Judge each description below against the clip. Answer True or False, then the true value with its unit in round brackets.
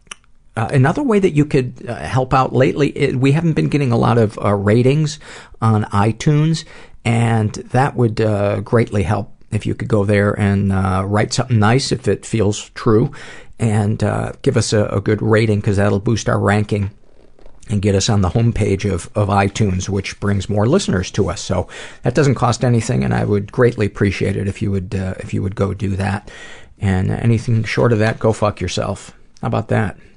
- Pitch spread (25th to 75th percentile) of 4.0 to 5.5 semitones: False (3.4 semitones)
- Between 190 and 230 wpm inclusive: True (205 wpm)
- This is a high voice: False (110 Hz)